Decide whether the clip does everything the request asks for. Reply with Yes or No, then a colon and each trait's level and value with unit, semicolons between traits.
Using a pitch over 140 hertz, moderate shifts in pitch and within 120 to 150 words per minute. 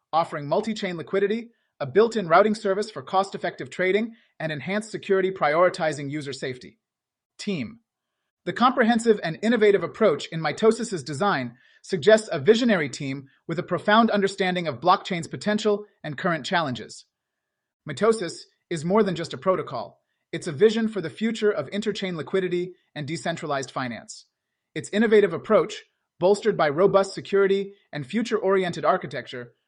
Yes: high, 190 Hz; average, 4.2 semitones; slow, 135 wpm